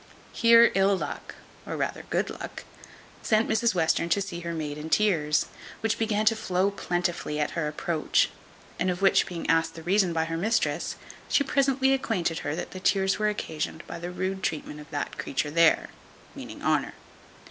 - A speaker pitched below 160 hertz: No, medium, 180 Hz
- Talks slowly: No, average, 180 wpm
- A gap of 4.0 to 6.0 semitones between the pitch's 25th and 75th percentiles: Yes, average, 4.5 semitones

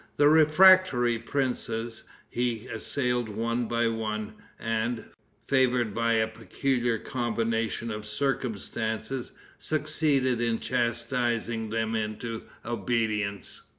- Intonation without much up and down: Yes, narrow, 1.9 semitones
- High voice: No, low, 115 Hz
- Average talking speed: No, slow, 95 wpm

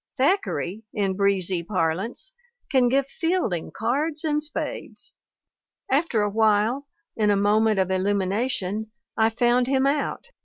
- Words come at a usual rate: No, slow, 130 wpm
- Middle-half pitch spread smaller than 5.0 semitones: No, wide, 5.5 semitones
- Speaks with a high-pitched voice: Yes, high, 220 Hz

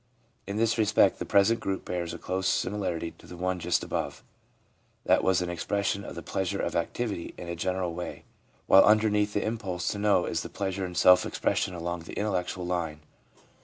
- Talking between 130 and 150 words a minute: No, average, 195 wpm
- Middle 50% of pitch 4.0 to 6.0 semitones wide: No, average, 2.7 semitones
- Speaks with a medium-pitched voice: No, very low, 95 Hz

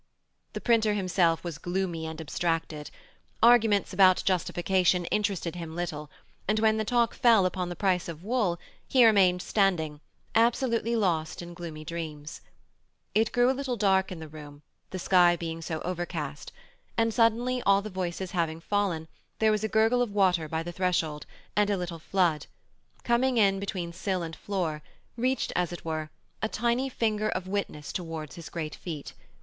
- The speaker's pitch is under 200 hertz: Yes, medium, 185 Hz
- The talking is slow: No, average, 170 wpm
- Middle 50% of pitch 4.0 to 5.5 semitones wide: Yes, average, 4.6 semitones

